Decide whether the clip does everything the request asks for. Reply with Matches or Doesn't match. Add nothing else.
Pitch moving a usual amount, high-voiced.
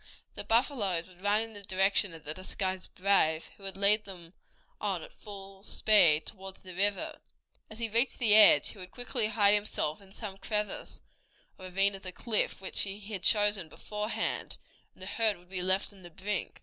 Doesn't match